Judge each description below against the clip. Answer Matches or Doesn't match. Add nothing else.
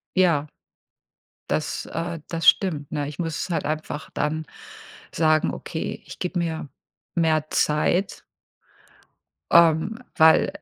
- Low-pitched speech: Doesn't match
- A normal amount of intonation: Doesn't match